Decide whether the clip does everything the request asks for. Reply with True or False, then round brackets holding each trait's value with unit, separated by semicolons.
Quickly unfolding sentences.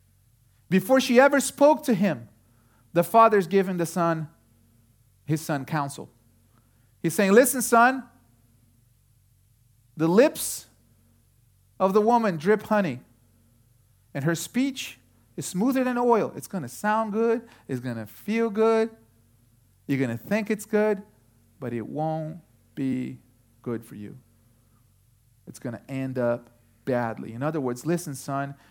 False (140 wpm)